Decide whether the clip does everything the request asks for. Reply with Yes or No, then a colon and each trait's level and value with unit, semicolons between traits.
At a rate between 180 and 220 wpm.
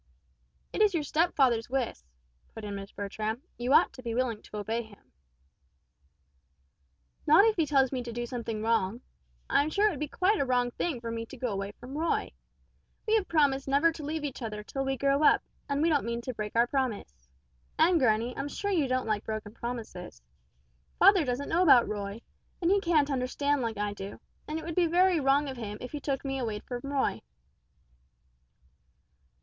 Yes: average, 200 wpm